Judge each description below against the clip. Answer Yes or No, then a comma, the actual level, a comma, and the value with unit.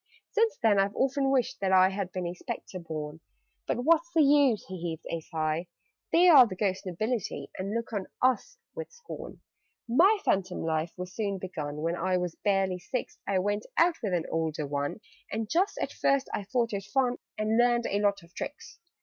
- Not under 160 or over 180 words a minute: No, average, 200 wpm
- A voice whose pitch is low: No, high, 200 Hz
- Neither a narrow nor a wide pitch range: No, wide, 6.0 semitones